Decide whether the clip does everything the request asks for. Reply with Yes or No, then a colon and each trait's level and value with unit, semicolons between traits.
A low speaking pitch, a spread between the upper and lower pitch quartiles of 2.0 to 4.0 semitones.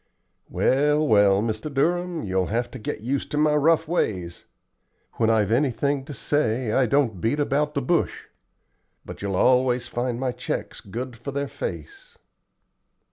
No: low, 130 Hz; average, 4.9 semitones